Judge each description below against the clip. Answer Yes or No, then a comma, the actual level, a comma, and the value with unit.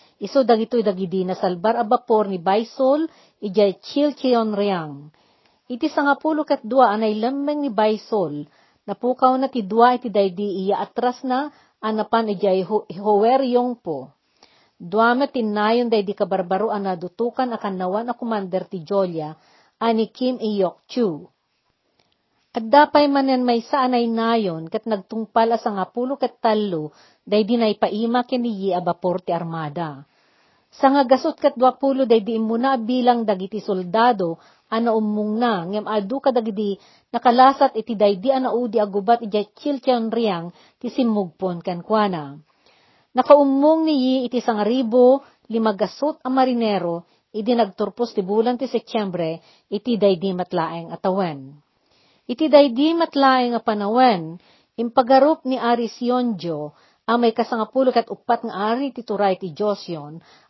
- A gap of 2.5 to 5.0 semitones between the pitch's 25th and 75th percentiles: Yes, average, 4.1 semitones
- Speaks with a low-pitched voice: No, high, 225 Hz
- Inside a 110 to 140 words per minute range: Yes, average, 135 wpm